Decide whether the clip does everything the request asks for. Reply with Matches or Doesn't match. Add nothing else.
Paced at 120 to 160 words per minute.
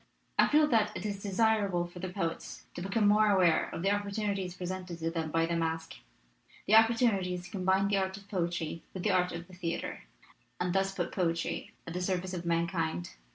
Doesn't match